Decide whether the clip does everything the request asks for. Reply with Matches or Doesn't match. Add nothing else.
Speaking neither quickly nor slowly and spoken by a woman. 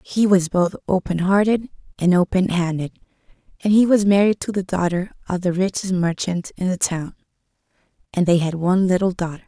Matches